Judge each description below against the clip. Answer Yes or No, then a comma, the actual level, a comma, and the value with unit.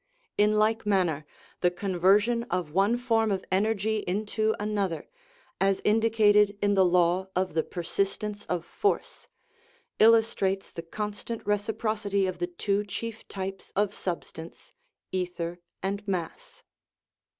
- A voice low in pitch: No, high, 200 Hz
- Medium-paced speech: No, slow, 125 wpm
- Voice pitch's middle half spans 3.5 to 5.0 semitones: No, average, 2.7 semitones